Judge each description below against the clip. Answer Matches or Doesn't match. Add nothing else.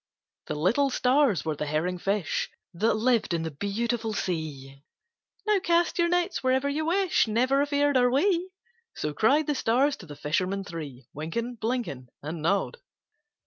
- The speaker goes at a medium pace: Matches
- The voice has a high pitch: Matches